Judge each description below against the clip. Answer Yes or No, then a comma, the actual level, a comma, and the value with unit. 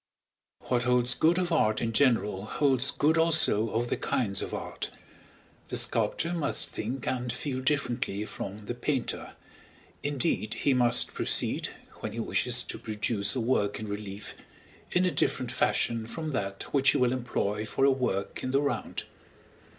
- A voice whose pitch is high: No, low, 125 Hz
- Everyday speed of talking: Yes, average, 165 wpm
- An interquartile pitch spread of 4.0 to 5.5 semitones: Yes, average, 4.4 semitones